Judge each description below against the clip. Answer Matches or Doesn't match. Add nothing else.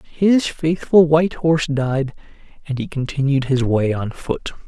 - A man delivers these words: Matches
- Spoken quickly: Doesn't match